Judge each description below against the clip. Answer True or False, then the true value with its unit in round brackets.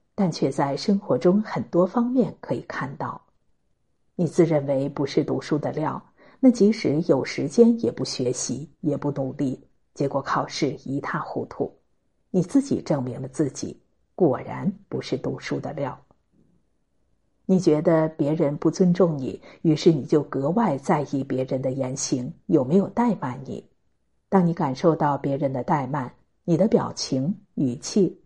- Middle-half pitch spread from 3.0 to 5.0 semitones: False (5.5 semitones)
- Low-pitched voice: False (160 Hz)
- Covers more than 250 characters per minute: False (225 characters per minute)